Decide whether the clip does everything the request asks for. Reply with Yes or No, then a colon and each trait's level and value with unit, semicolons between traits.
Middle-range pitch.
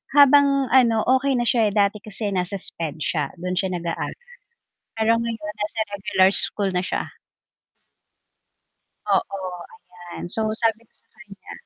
No: high, 210 Hz